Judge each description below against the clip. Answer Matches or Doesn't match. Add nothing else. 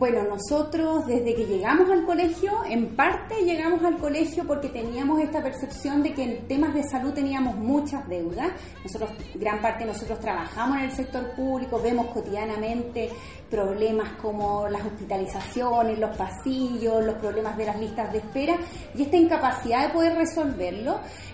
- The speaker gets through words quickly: Doesn't match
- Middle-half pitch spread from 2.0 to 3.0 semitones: Doesn't match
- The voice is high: Matches